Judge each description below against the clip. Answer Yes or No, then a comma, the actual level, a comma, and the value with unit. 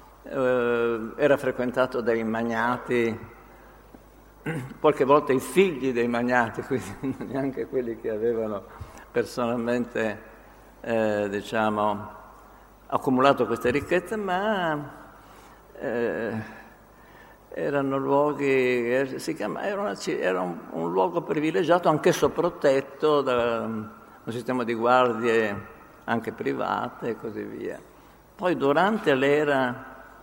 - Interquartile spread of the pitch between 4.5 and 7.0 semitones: No, average, 3.3 semitones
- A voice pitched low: Yes, low, 125 Hz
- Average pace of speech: No, slow, 100 wpm